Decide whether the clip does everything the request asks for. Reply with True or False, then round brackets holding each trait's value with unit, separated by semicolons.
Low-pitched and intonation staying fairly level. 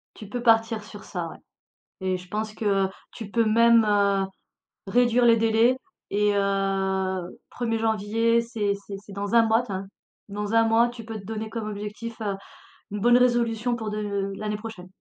False (215 Hz; 2.3 semitones)